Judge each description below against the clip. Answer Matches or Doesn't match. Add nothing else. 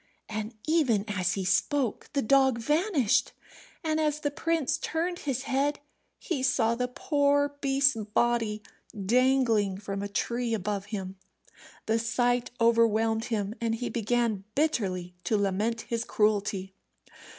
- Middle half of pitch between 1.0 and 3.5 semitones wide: Doesn't match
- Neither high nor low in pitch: Doesn't match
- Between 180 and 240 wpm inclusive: Doesn't match